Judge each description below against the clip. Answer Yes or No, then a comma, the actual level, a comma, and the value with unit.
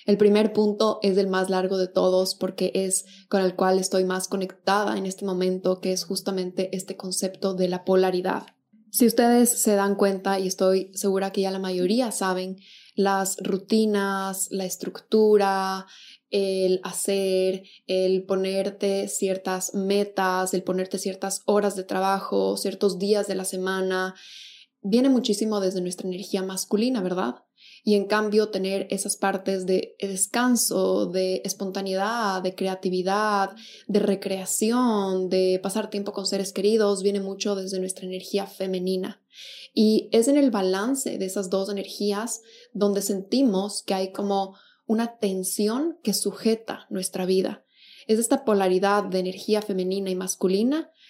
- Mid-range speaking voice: No, high, 195 Hz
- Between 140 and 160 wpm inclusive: Yes, average, 145 wpm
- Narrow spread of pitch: Yes, narrow, 1.6 semitones